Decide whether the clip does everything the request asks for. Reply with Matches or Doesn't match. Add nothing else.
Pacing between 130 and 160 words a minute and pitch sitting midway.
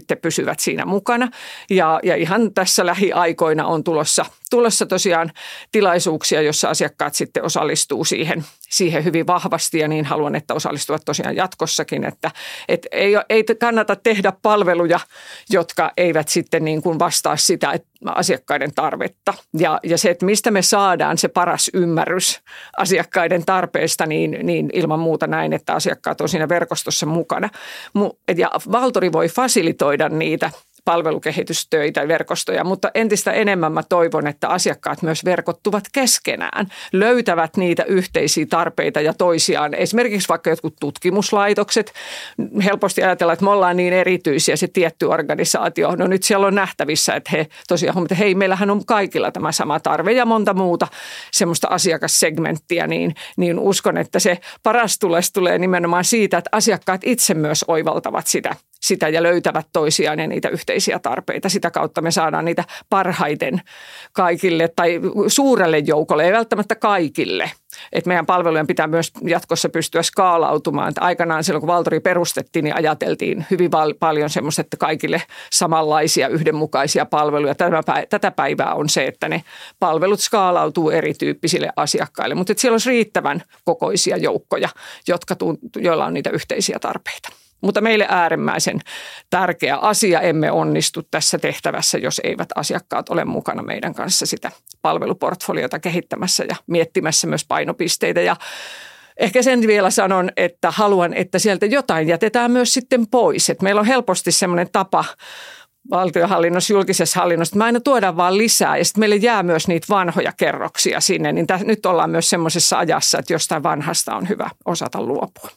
Matches